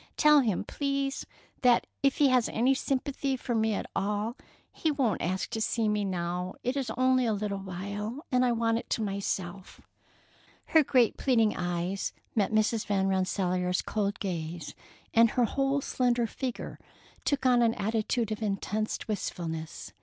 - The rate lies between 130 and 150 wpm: No, average, 160 wpm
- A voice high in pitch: Yes, high, 220 Hz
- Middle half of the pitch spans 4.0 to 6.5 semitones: Yes, average, 4.5 semitones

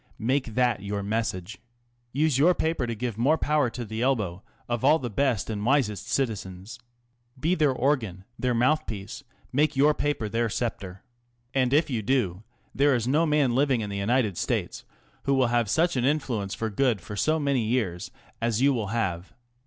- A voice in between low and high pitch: No, low, 120 Hz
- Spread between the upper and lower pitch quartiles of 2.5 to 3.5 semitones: No, average, 4.6 semitones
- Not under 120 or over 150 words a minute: No, average, 185 wpm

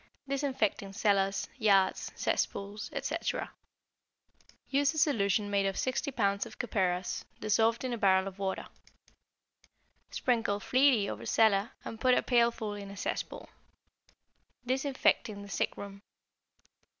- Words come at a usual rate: No, slow, 125 wpm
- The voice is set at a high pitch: Yes, high, 210 Hz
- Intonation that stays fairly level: No, average, 3.8 semitones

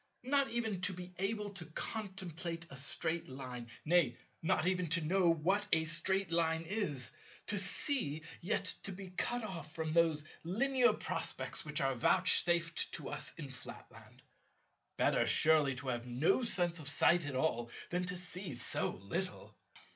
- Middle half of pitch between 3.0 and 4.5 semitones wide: Yes, average, 3.9 semitones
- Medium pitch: Yes, medium, 170 Hz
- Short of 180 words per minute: Yes, average, 160 wpm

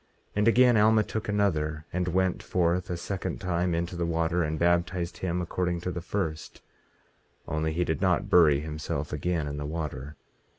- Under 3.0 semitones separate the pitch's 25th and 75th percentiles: Yes, narrow, 2.6 semitones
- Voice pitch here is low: Yes, very low, 85 Hz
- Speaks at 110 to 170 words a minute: No, average, 180 wpm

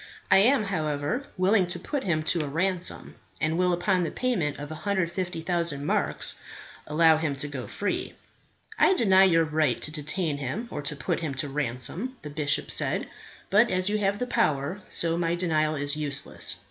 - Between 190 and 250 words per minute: No, average, 180 wpm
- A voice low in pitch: No, medium, 165 Hz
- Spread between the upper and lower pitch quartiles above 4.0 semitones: Yes, average, 4.4 semitones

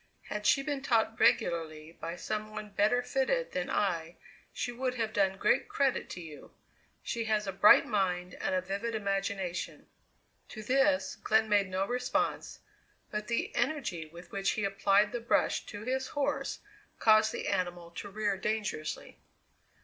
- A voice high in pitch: Yes, high, 210 Hz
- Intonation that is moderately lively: Yes, average, 3.8 semitones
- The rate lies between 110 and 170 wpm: Yes, average, 160 wpm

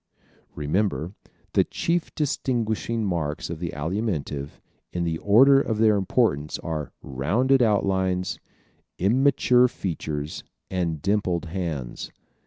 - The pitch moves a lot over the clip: Yes, wide, 5.9 semitones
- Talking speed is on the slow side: Yes, slow, 105 wpm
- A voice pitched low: Yes, very low, 95 Hz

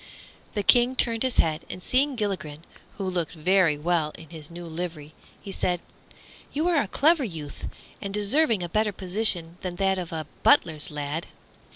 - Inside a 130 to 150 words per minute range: No, average, 175 wpm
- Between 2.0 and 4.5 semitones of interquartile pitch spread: No, average, 4.9 semitones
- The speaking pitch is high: No, medium, 180 Hz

